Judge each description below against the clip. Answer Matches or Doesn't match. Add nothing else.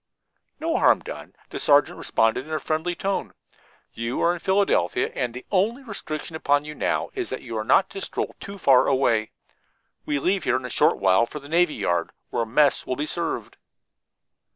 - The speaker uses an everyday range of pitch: Doesn't match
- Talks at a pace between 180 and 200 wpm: Matches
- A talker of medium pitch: Matches